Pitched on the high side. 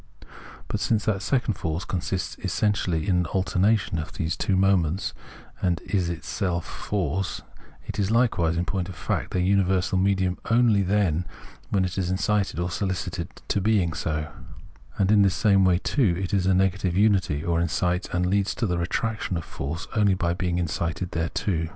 No: very low, 95 Hz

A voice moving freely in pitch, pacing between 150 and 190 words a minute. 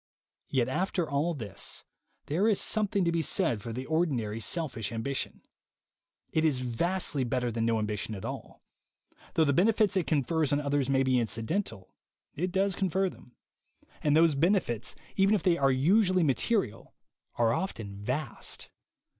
Yes: wide, 7.1 semitones; average, 155 wpm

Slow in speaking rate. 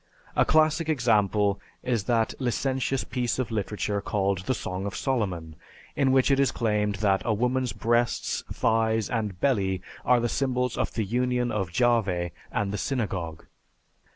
No: average, 155 wpm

